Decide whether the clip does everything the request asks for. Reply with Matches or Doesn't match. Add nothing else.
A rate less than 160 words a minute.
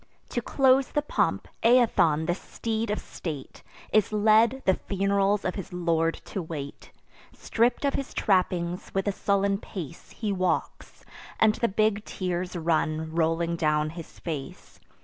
Matches